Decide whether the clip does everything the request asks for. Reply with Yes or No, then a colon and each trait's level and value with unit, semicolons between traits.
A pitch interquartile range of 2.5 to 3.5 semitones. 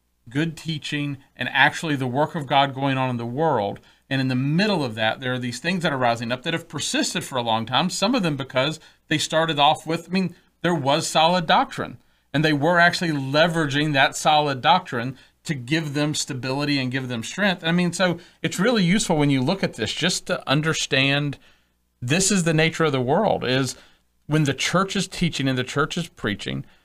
No: average, 4.3 semitones